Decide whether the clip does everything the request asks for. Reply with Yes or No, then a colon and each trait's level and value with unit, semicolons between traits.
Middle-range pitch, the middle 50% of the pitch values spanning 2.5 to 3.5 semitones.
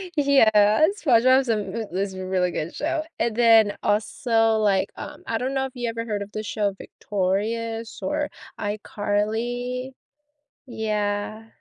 No: high, 220 Hz; average, 2.9 semitones